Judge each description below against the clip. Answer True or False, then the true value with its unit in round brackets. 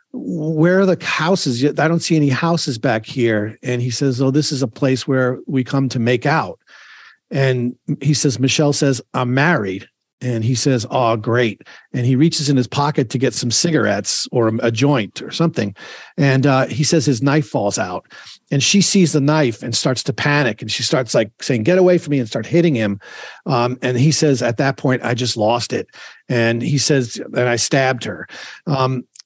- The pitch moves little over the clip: False (3.3 semitones)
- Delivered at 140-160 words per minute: False (205 wpm)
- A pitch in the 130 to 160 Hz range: True (135 Hz)